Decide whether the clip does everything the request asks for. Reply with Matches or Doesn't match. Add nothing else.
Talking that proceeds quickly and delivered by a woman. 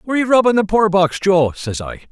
Doesn't match